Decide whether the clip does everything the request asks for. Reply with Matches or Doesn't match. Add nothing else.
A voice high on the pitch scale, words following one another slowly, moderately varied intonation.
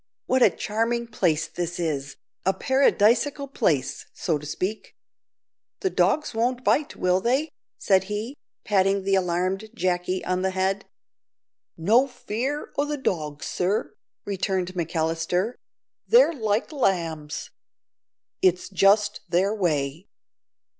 Matches